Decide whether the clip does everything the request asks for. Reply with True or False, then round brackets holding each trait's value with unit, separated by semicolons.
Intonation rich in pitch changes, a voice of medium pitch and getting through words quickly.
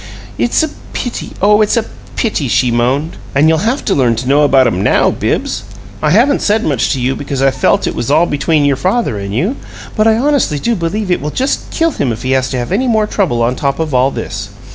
True (8.7 semitones; 150 Hz; 245 wpm)